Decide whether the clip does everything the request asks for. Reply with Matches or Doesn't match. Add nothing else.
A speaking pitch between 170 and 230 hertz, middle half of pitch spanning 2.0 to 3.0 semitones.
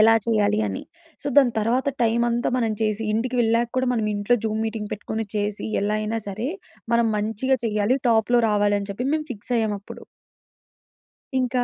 Matches